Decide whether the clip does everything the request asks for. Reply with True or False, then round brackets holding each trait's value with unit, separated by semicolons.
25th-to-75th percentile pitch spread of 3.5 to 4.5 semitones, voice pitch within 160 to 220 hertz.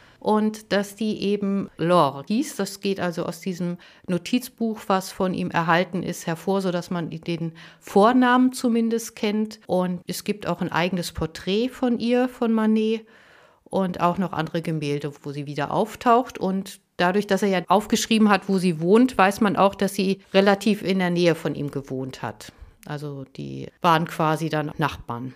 True (4.1 semitones; 185 Hz)